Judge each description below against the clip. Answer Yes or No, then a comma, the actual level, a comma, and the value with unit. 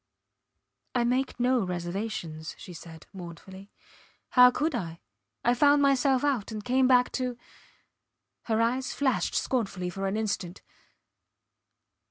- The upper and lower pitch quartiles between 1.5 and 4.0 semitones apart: No, wide, 5.6 semitones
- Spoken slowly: Yes, slow, 125 wpm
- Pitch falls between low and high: No, high, 230 Hz